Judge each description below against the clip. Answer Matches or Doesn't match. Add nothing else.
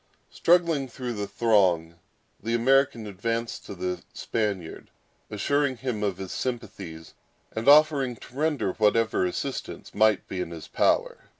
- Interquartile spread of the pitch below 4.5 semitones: Doesn't match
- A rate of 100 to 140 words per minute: Matches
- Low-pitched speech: Matches